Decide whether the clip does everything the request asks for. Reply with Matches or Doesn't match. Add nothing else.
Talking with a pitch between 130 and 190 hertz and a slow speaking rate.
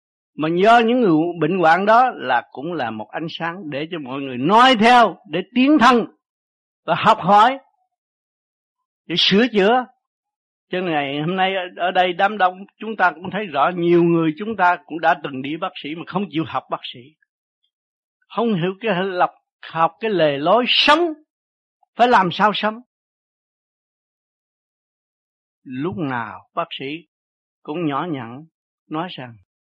Matches